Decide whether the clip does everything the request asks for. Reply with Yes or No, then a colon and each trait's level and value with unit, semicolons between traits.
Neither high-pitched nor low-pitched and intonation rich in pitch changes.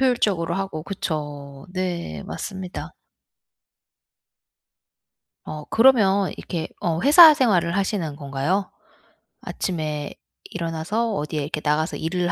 No: medium, 170 Hz; average, 4.4 semitones